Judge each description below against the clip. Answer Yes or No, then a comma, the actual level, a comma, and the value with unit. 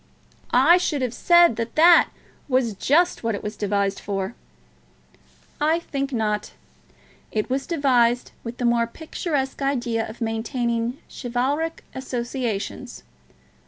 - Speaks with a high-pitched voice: Yes, high, 245 Hz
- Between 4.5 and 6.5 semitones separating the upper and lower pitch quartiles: No, average, 3.7 semitones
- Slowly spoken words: Yes, slow, 125 wpm